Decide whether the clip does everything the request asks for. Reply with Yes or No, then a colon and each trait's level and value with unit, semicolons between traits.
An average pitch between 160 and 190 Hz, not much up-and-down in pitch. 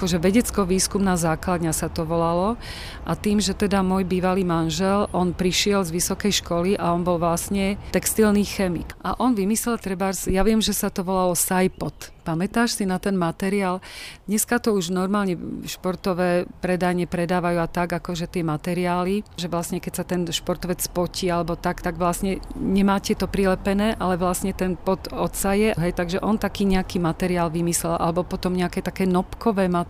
Yes: medium, 185 Hz; narrow, 2.0 semitones